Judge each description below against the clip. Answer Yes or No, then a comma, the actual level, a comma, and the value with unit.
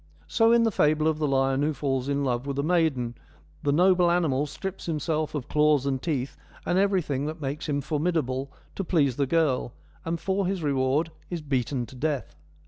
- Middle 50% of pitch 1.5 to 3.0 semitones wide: No, average, 3.6 semitones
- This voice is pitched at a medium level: Yes, medium, 150 Hz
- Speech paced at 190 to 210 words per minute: Yes, average, 195 wpm